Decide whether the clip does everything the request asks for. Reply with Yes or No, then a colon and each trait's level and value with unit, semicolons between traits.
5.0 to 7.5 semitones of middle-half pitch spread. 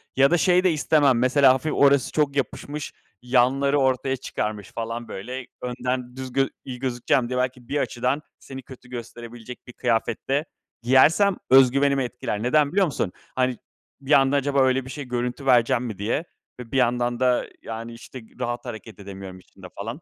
No: narrow, 2.4 semitones